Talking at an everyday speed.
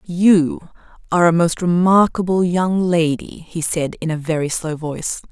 Yes: average, 160 wpm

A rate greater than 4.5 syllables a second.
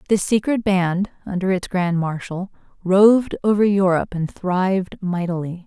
Yes: 4.7 syllables/s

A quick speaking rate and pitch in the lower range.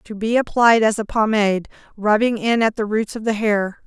No: fast, 220 wpm; high, 215 Hz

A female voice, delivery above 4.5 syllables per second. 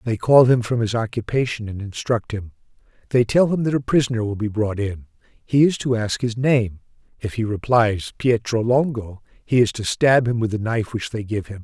No: male; 5.2 syllables/s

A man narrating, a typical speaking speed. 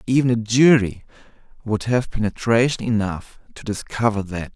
No: male; slow, 130 wpm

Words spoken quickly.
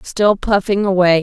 No: average, 145 wpm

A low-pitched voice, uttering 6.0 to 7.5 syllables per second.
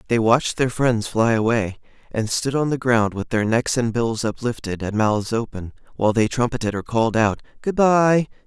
No: low, 120 Hz; 5.0 syllables/s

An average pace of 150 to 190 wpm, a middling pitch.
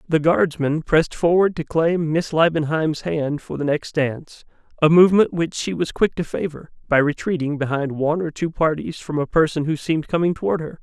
No: average, 200 wpm; medium, 160 Hz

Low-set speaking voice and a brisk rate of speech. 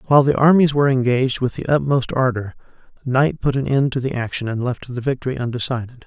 Yes: low, 130 Hz; fast, 210 wpm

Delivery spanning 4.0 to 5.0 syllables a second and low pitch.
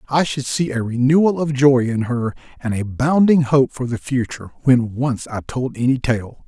Yes: 4.7 syllables/s; low, 130 Hz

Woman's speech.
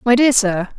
Yes: female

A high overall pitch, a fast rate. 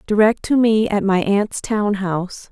No: high, 205 Hz; average, 190 wpm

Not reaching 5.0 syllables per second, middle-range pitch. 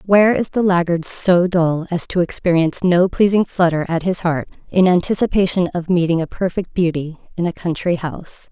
No: 5.2 syllables/s; medium, 175 Hz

